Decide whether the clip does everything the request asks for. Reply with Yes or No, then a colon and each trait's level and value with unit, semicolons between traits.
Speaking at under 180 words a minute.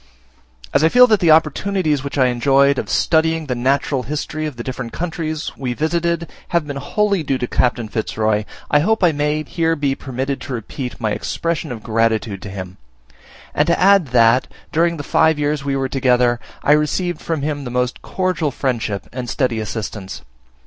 No: average, 190 wpm